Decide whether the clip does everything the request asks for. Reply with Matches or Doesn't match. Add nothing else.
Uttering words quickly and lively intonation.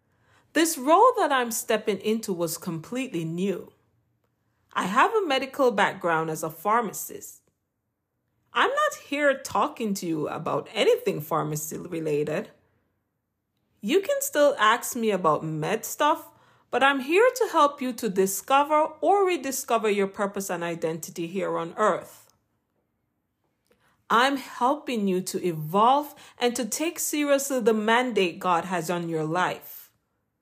Doesn't match